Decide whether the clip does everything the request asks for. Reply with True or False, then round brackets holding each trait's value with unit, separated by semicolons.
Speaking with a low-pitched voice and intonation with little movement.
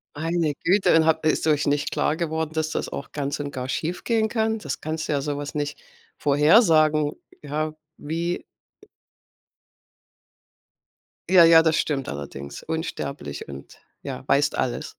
False (155 Hz; 2.1 semitones)